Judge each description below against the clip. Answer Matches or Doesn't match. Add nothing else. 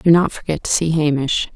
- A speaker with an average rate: Doesn't match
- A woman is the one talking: Matches